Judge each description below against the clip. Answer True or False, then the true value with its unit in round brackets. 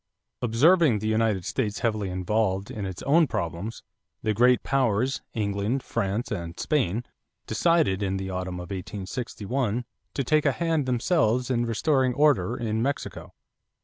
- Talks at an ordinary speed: True (145 wpm)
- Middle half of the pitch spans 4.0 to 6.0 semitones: True (5.0 semitones)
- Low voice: True (115 Hz)